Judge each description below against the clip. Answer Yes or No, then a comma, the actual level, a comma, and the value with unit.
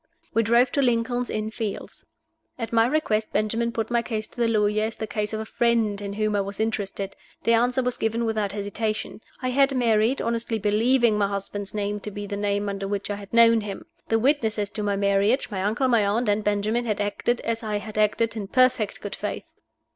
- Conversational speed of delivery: No, fast, 215 wpm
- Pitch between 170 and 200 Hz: No, high, 215 Hz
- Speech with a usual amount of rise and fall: No, narrow, 2.2 semitones